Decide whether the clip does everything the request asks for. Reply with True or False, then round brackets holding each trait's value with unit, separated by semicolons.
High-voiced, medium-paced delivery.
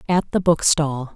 False (155 Hz; 155 wpm)